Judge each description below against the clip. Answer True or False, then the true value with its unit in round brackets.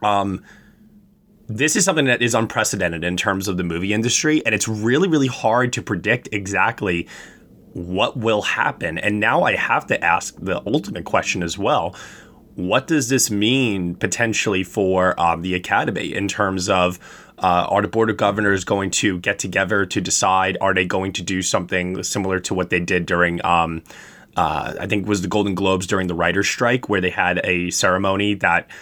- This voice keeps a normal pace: True (185 wpm)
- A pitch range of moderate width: True (3.3 semitones)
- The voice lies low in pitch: True (100 Hz)